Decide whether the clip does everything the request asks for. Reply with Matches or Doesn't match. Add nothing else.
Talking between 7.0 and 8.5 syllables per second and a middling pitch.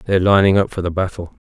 Doesn't match